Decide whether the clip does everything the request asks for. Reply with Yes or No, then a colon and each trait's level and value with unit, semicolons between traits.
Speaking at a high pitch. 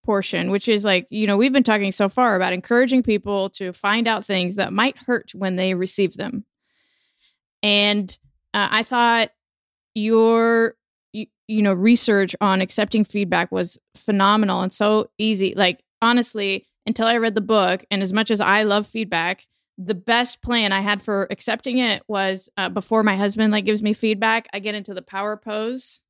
Yes: high, 210 Hz